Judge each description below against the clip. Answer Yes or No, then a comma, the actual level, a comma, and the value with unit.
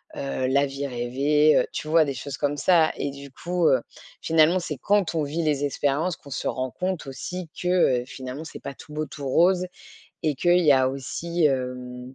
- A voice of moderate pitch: Yes, medium, 145 Hz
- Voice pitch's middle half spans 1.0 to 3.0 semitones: No, average, 3.8 semitones